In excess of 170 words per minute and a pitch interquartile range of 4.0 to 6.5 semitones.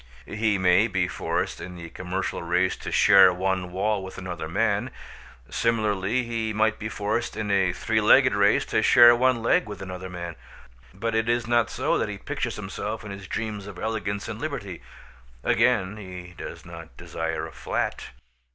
No: average, 180 wpm; average, 3.4 semitones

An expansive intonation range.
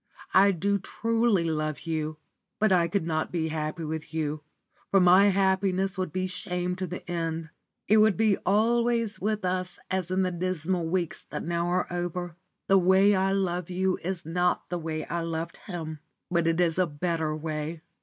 No: average, 2.7 semitones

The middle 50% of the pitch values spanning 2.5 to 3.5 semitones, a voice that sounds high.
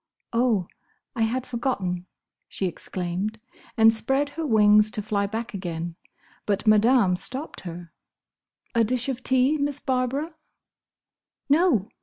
No: average, 4.5 semitones; high, 225 Hz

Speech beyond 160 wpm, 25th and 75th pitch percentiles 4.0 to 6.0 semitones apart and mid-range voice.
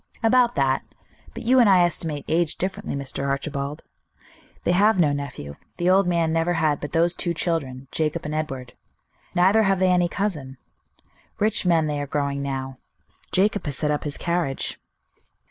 Yes: average, 170 wpm; average, 4.3 semitones; medium, 160 Hz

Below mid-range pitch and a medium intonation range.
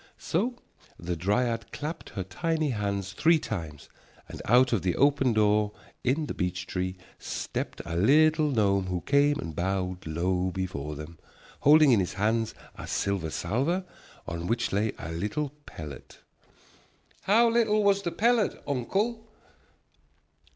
No: low, 110 Hz; wide, 8.7 semitones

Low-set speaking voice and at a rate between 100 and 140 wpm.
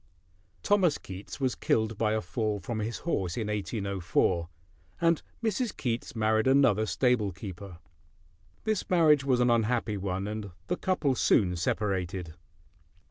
Yes: low, 110 Hz; slow, 135 wpm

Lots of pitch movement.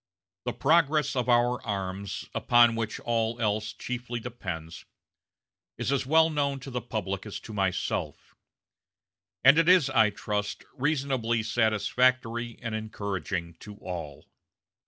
No: average, 3.8 semitones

